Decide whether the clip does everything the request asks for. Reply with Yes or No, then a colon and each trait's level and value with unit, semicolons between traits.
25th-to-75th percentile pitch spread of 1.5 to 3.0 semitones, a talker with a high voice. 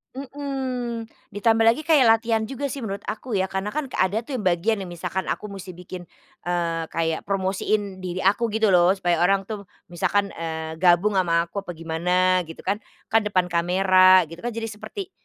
No: average, 4.1 semitones; high, 195 Hz